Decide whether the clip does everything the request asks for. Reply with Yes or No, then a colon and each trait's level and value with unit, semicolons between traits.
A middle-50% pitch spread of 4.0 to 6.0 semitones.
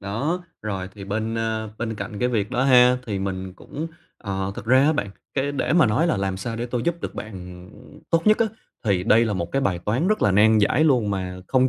Yes: average, 4.9 semitones